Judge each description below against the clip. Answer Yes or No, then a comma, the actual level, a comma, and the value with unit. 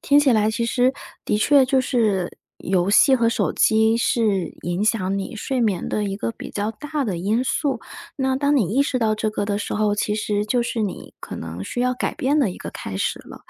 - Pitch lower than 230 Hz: Yes, high, 220 Hz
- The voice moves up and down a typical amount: Yes, average, 3.8 semitones